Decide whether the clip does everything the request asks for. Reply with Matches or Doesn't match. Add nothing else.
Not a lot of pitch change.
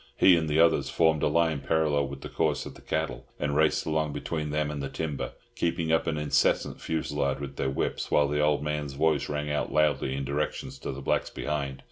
Matches